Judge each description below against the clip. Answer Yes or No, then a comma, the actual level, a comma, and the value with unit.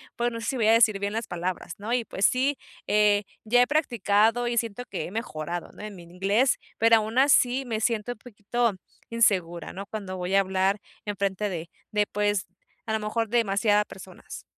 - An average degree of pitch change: Yes, average, 3.0 semitones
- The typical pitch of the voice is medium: No, high, 210 Hz